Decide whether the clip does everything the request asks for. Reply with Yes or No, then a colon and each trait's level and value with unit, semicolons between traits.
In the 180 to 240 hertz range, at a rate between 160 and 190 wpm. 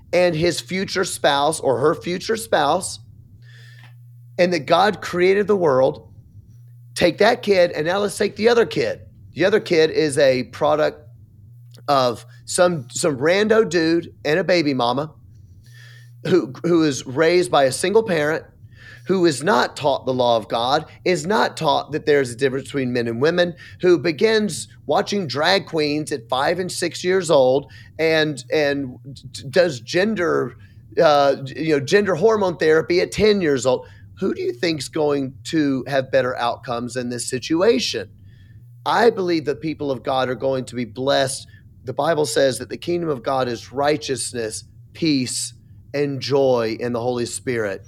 No: medium, 140 Hz; average, 165 wpm